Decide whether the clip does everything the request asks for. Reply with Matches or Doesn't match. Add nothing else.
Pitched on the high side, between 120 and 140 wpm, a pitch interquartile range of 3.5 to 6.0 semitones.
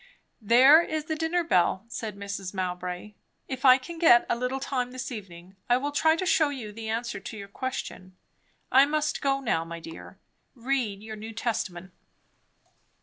Doesn't match